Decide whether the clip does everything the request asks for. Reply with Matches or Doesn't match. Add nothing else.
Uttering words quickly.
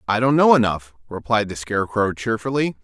Doesn't match